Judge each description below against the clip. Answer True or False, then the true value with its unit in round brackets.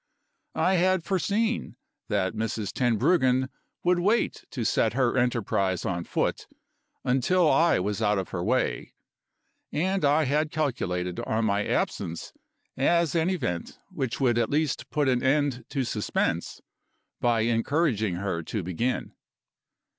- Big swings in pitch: True (6.8 semitones)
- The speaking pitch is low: True (125 Hz)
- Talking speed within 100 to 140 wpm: True (135 wpm)